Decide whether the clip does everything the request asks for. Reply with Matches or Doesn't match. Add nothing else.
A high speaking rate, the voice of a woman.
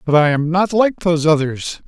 Doesn't match